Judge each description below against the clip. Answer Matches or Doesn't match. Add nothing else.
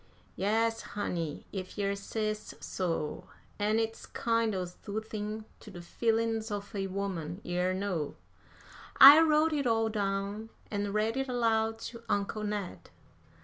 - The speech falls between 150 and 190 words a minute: Doesn't match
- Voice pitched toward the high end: Matches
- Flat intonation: Matches